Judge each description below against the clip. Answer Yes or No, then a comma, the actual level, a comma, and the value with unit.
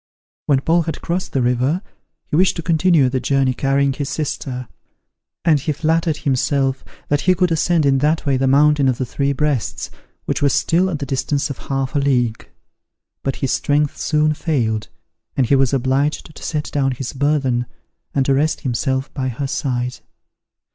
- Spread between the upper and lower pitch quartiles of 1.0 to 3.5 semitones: Yes, narrow, 2.5 semitones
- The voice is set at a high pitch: No, medium, 140 Hz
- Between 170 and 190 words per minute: Yes, average, 180 wpm